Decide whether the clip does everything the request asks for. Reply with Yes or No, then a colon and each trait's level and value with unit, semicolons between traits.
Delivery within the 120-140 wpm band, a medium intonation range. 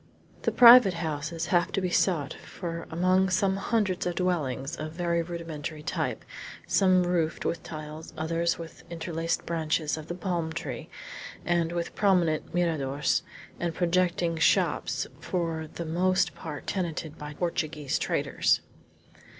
No: slow, 135 wpm; narrow, 2.2 semitones